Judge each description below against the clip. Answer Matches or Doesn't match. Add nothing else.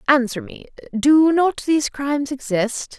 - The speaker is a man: Doesn't match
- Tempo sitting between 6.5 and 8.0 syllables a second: Doesn't match